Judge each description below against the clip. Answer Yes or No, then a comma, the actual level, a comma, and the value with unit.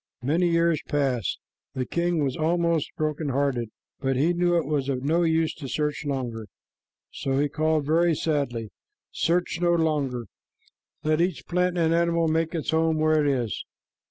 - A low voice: No, medium, 155 Hz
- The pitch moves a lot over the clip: No, average, 3.4 semitones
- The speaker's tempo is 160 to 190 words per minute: Yes, average, 165 wpm